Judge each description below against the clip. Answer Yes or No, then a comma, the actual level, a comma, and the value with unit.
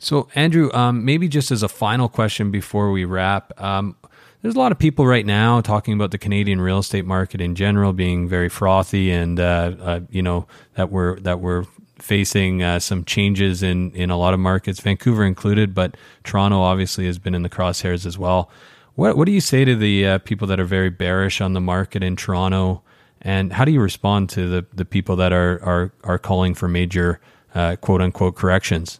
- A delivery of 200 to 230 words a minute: Yes, fast, 205 wpm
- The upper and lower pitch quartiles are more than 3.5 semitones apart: No, narrow, 2.5 semitones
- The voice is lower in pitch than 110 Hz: Yes, very low, 95 Hz